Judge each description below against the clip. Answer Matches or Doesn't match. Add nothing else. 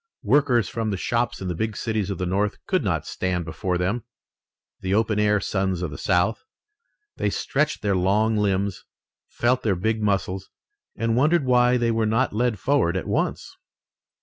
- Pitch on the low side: Matches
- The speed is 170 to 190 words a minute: Matches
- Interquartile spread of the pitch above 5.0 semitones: Doesn't match